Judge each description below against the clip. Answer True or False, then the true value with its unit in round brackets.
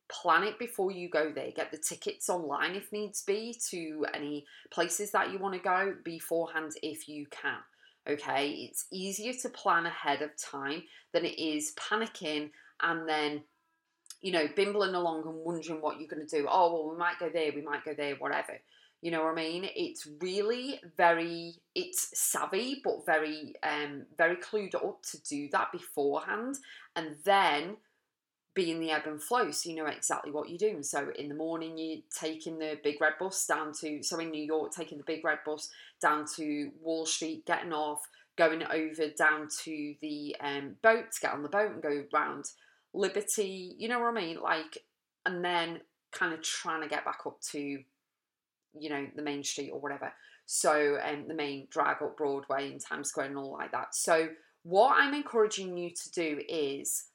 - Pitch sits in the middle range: True (160 Hz)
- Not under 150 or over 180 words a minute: False (195 wpm)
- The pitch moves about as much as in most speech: True (4.1 semitones)